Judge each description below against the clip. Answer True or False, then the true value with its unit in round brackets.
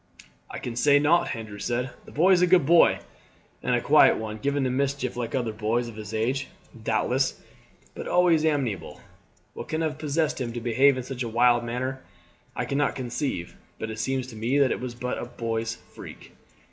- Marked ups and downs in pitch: False (3.5 semitones)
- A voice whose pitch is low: True (125 Hz)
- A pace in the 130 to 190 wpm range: False (200 wpm)